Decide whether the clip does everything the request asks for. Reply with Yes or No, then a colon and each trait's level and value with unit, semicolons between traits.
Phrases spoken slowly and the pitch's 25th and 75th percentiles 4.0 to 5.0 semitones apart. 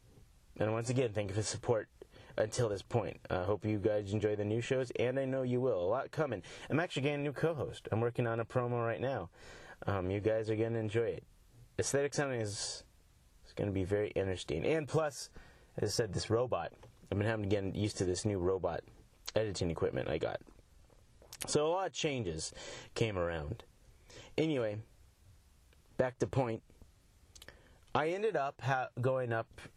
No: average, 190 wpm; average, 4.4 semitones